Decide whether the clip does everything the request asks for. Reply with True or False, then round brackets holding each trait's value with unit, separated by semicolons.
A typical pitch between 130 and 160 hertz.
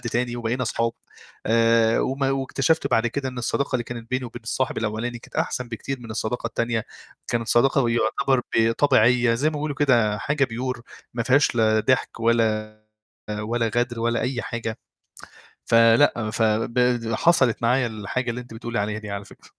False (120 Hz)